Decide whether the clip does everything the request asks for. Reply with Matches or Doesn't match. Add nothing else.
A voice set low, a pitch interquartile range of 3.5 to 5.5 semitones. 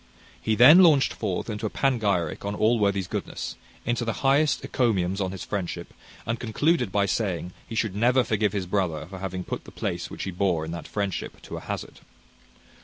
Matches